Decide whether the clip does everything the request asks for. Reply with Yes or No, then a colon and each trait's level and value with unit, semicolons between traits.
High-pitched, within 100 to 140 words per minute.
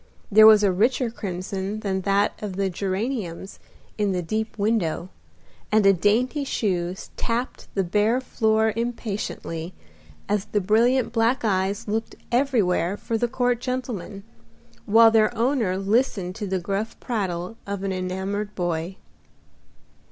Yes: high, 210 Hz; slow, 135 wpm